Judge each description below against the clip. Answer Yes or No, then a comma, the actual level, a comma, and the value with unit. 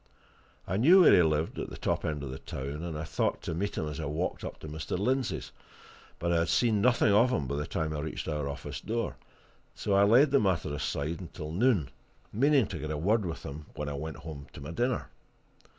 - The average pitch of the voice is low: Yes, very low, 80 Hz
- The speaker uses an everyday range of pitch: No, wide, 6.1 semitones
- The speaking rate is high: Yes, fast, 235 wpm